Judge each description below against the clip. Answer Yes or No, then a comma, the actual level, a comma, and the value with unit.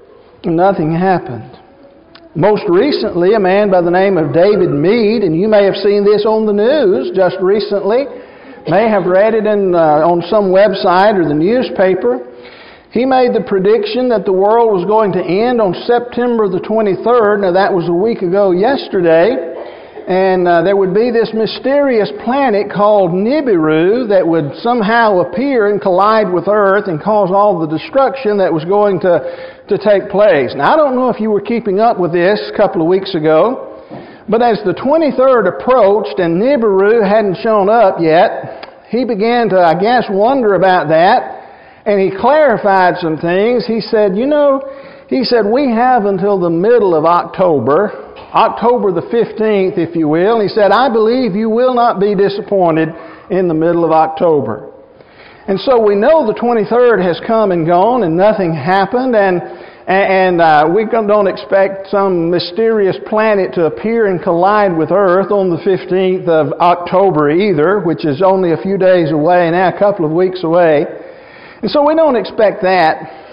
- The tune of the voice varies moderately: Yes, average, 3.6 semitones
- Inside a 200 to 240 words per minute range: No, average, 175 wpm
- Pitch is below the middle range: No, high, 200 Hz